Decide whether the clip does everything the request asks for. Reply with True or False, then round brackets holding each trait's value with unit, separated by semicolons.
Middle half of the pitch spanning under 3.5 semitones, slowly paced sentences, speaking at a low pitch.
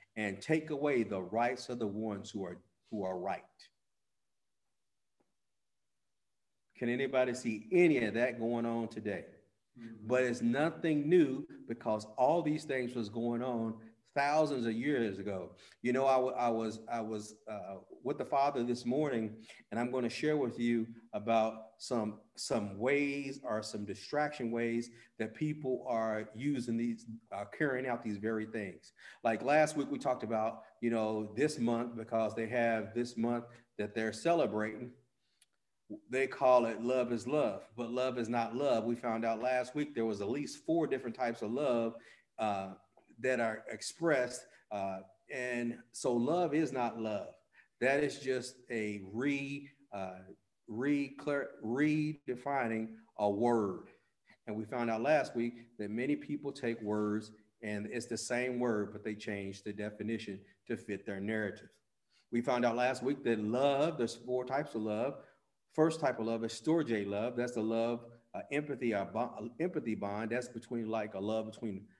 False (2.7 semitones; 165 wpm; 115 Hz)